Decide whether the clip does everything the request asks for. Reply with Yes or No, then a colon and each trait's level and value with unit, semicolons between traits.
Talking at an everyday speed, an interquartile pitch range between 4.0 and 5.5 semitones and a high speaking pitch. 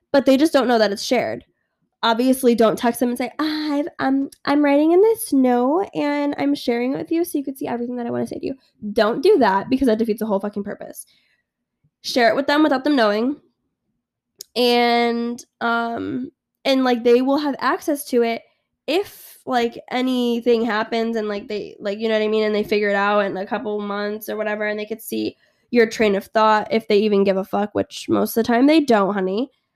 No: fast, 230 wpm; average, 4.5 semitones; high, 235 Hz